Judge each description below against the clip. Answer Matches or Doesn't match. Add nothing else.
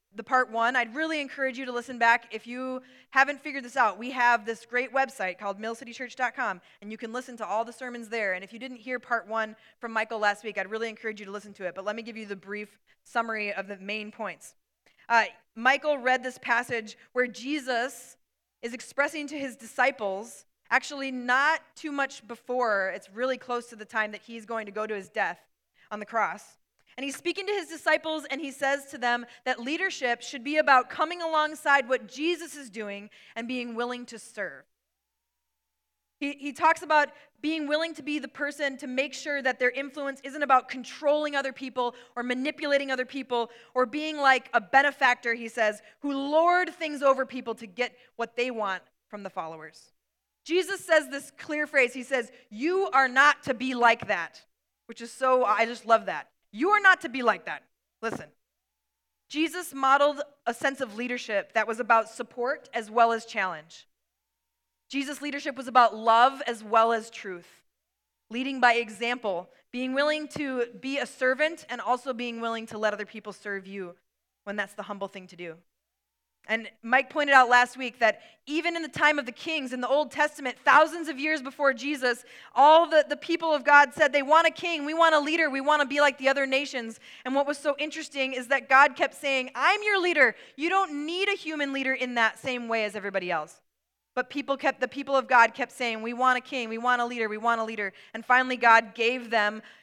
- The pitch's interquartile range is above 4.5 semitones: Doesn't match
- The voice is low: Doesn't match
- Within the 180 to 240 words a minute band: Matches